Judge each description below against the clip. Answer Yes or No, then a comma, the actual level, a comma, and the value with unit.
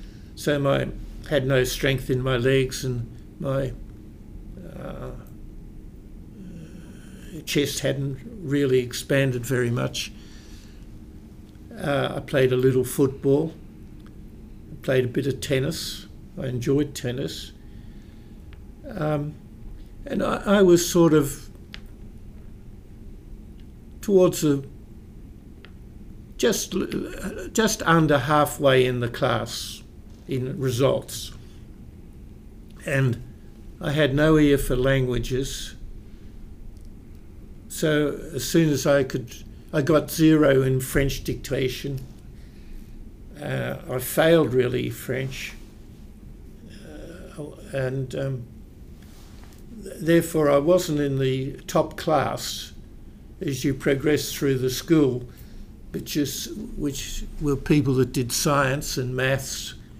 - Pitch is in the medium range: No, low, 130 Hz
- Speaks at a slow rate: Yes, slow, 100 wpm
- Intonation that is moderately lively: Yes, average, 4.8 semitones